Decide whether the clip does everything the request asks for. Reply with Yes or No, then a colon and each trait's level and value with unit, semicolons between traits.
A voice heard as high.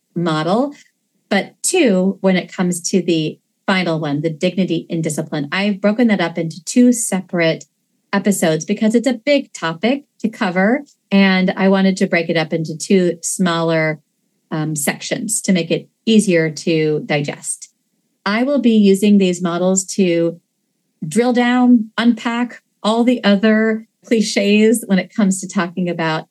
Yes: high, 195 Hz